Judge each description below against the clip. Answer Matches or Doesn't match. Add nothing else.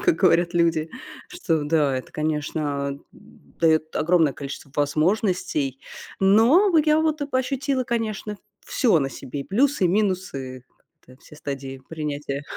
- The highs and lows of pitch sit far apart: Matches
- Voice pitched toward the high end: Doesn't match